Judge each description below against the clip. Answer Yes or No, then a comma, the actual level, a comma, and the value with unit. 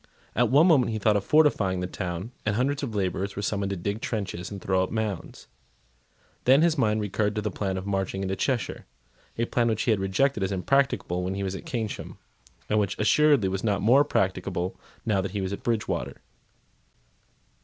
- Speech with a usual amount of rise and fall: Yes, average, 3.5 semitones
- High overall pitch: No, low, 105 Hz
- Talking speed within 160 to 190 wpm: No, average, 200 wpm